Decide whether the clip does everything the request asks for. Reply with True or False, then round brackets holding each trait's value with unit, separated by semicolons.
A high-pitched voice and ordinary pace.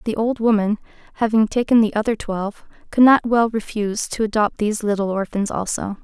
True (215 Hz; 180 wpm)